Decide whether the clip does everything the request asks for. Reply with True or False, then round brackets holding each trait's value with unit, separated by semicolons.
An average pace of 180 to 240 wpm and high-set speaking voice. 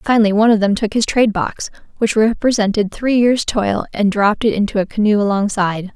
True (200 wpm; 210 Hz)